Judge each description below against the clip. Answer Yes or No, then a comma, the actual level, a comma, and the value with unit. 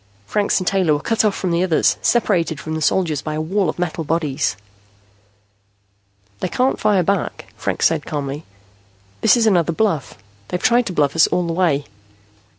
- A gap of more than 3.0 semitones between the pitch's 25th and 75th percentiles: Yes, average, 4.2 semitones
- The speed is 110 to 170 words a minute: No, average, 180 wpm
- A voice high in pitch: No, medium, 170 Hz